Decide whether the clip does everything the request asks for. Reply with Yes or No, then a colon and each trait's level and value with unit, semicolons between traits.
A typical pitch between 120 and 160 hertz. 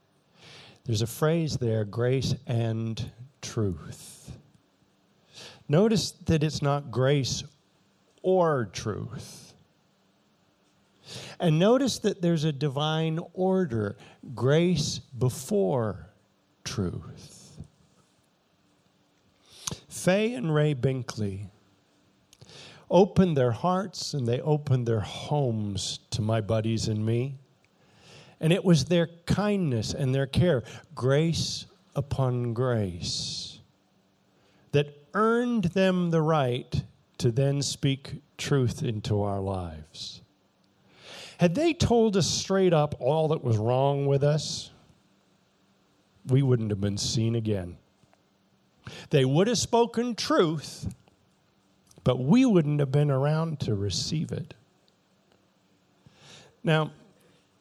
Yes: medium, 140 Hz